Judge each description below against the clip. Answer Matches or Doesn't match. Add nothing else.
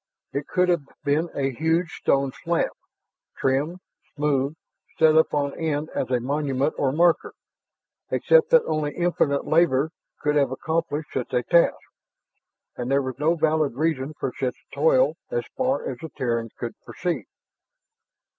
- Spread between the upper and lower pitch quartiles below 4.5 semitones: Matches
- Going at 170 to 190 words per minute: Doesn't match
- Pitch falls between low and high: Matches